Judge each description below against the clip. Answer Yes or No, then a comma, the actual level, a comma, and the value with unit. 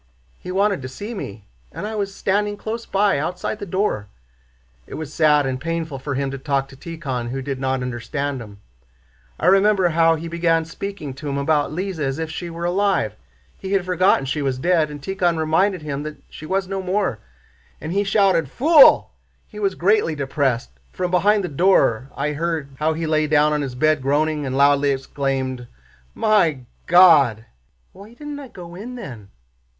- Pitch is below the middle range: No, medium, 160 Hz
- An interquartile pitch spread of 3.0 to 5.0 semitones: No, wide, 5.6 semitones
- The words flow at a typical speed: Yes, average, 185 wpm